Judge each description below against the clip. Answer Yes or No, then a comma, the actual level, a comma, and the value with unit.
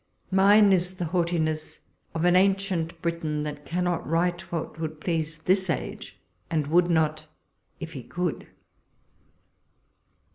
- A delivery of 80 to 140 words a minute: Yes, slow, 135 wpm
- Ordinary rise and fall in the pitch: No, narrow, 2.3 semitones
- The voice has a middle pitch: Yes, medium, 170 Hz